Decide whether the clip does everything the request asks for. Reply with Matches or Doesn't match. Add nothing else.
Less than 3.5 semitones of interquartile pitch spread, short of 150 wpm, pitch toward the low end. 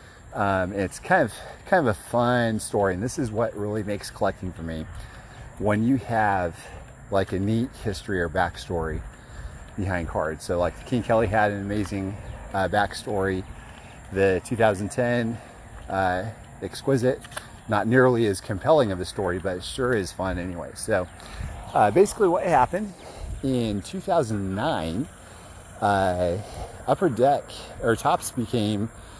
Doesn't match